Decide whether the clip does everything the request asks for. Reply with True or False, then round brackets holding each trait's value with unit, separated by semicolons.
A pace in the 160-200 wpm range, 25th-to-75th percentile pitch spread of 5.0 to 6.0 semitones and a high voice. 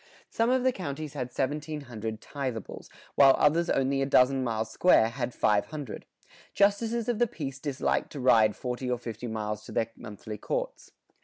False (165 wpm; 5.3 semitones; 135 Hz)